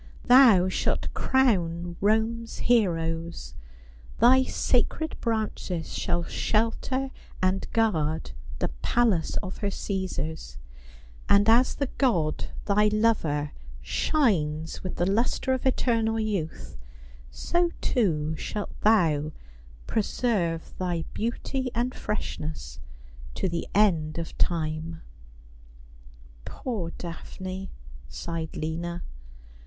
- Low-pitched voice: No, medium, 185 Hz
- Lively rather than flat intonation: Yes, wide, 5.8 semitones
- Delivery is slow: Yes, slow, 100 wpm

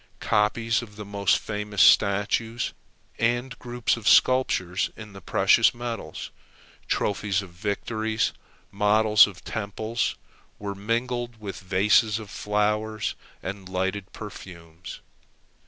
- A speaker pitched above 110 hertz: No, low, 105 Hz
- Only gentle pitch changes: Yes, narrow, 2.3 semitones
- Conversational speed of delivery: No, slow, 110 wpm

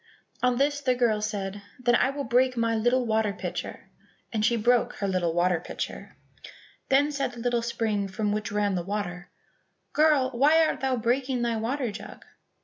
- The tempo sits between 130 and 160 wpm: No, average, 180 wpm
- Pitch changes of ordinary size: Yes, average, 3.7 semitones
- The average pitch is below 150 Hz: No, high, 235 Hz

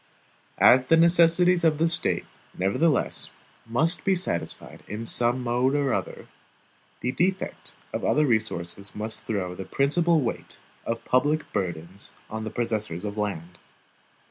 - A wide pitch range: Yes, wide, 7.4 semitones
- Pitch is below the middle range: Yes, low, 120 Hz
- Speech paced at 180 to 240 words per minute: No, average, 140 wpm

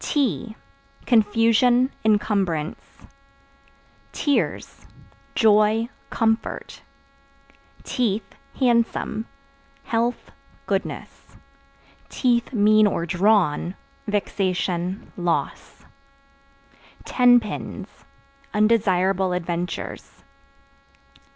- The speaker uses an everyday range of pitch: Yes, average, 3.9 semitones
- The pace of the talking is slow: Yes, slow, 55 wpm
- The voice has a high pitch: Yes, high, 210 Hz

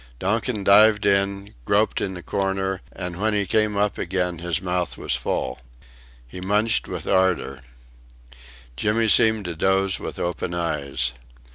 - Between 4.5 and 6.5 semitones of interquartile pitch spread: No, average, 2.8 semitones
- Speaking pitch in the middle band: No, very low, 95 Hz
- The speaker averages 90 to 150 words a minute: Yes, average, 145 wpm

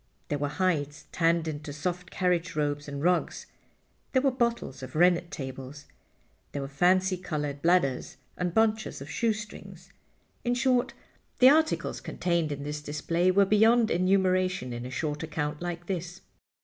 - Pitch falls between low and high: Yes, medium, 170 Hz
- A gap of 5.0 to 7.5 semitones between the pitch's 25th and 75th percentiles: No, average, 4.3 semitones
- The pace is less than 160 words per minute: Yes, average, 150 wpm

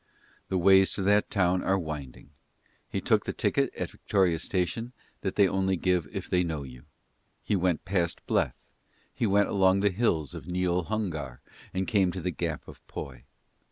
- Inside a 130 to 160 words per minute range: No, average, 180 wpm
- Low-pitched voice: Yes, very low, 95 Hz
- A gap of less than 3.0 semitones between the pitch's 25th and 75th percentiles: Yes, narrow, 2.4 semitones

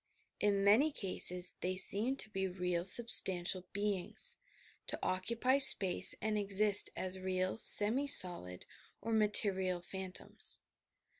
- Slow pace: Yes, slow, 125 wpm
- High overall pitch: Yes, high, 195 Hz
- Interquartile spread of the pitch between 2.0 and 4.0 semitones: Yes, narrow, 2.6 semitones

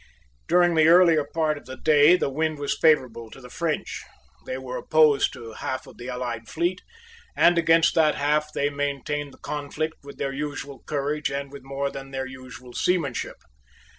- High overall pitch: No, medium, 145 Hz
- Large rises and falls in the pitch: No, average, 2.8 semitones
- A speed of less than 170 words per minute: No, average, 180 wpm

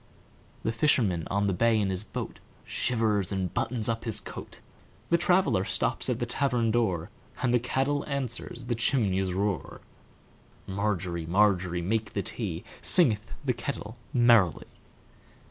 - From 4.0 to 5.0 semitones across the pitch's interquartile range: Yes, average, 4.3 semitones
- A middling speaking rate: No, slow, 125 wpm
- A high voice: No, low, 110 Hz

